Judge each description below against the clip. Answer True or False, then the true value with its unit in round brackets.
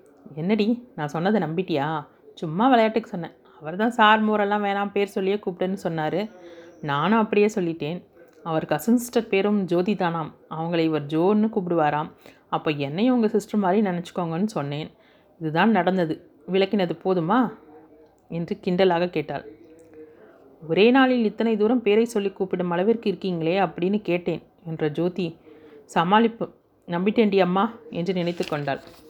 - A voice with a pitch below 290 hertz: True (185 Hz)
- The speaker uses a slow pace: False (130 wpm)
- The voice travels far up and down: False (4.4 semitones)